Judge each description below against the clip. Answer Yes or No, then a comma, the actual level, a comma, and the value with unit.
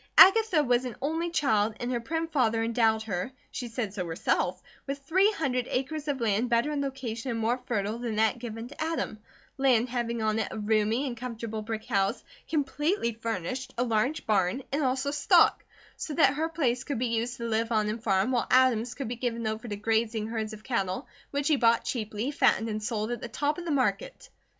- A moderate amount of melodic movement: Yes, average, 3.7 semitones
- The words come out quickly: Yes, fast, 210 wpm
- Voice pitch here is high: Yes, high, 235 Hz